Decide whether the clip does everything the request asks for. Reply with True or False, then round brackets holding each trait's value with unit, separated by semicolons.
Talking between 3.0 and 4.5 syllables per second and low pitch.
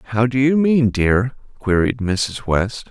True (3.8 syllables/s; 120 Hz)